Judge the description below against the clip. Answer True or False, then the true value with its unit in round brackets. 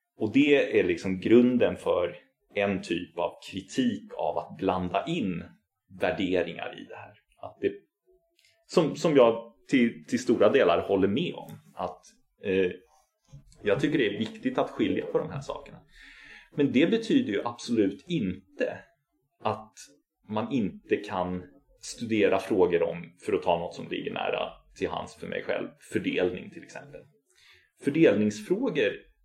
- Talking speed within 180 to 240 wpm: False (150 wpm)